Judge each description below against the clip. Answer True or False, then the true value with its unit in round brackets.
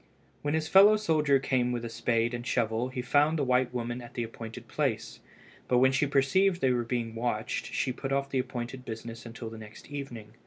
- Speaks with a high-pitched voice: False (125 Hz)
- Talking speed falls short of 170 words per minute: False (205 wpm)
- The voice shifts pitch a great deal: False (2.9 semitones)